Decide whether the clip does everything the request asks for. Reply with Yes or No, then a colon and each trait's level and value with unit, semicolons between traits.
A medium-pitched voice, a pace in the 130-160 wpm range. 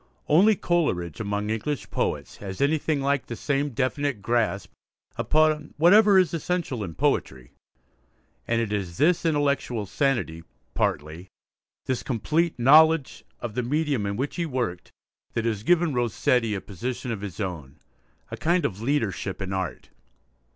No: low, 125 Hz; average, 145 wpm